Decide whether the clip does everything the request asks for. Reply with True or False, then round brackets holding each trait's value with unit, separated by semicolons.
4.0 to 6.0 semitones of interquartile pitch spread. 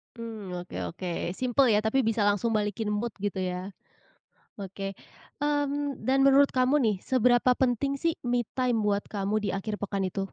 True (4.4 semitones)